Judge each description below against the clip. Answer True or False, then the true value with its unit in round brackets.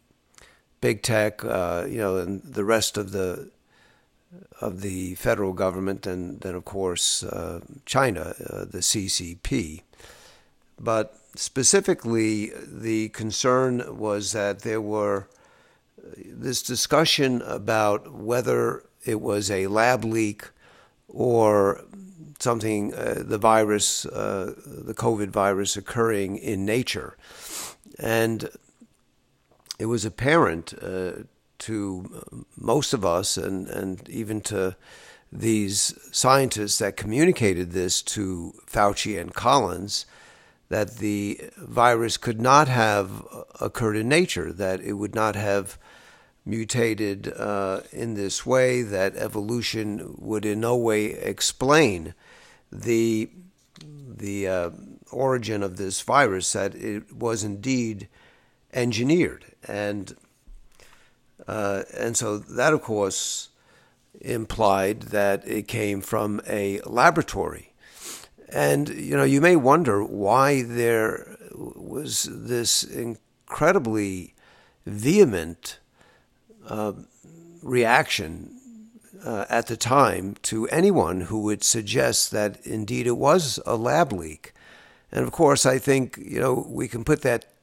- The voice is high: False (110 Hz)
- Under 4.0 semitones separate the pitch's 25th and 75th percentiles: True (3.2 semitones)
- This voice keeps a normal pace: False (115 wpm)